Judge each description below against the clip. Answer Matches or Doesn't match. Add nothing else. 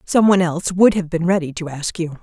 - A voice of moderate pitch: Matches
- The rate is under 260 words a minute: Doesn't match